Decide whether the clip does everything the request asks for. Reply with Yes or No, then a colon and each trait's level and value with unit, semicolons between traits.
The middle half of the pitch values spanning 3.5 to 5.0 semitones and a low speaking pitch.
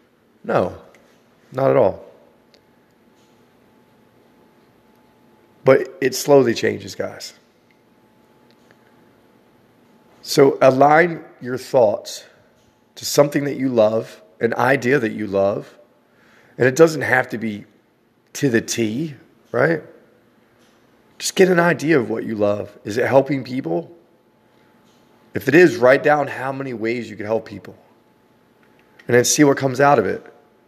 Yes: average, 4.3 semitones; low, 125 Hz